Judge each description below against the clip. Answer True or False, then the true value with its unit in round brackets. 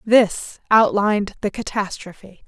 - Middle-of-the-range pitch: False (205 Hz)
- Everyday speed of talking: False (95 wpm)